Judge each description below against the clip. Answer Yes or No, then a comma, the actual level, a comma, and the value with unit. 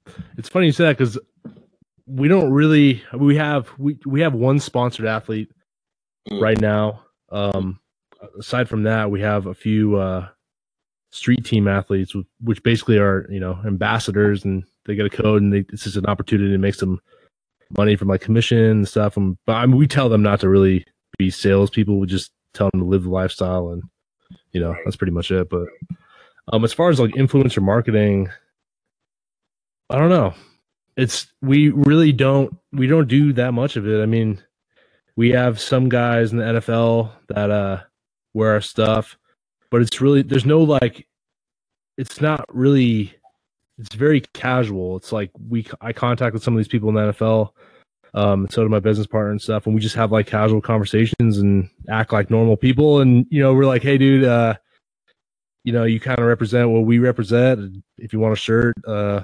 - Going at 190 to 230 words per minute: Yes, average, 195 wpm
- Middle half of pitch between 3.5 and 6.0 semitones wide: Yes, average, 3.8 semitones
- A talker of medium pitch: No, low, 110 Hz